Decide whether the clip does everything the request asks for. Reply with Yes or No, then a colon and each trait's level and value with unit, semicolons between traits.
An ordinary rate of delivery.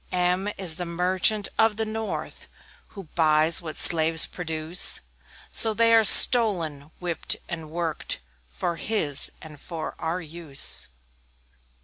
No: slow, 130 wpm